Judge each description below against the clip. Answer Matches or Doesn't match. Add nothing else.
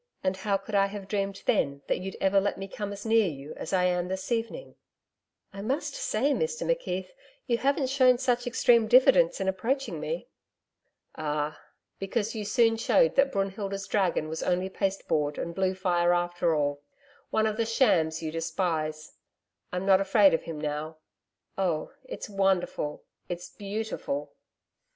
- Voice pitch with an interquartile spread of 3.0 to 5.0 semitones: Matches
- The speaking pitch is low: Doesn't match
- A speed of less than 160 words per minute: Doesn't match